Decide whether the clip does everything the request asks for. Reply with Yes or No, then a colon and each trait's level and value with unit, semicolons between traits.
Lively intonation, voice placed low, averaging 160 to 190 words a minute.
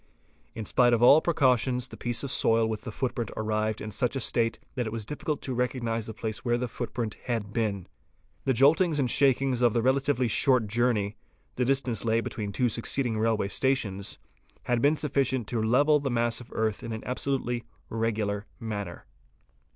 No: average, 2.8 semitones; low, 120 Hz; average, 180 wpm